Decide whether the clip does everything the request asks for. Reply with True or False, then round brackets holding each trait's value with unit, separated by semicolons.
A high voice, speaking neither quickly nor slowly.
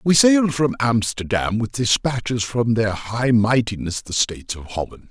False (115 Hz; 165 wpm)